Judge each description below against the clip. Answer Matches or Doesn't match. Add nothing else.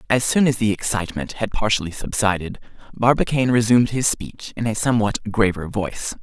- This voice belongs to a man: Matches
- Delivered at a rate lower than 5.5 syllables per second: Doesn't match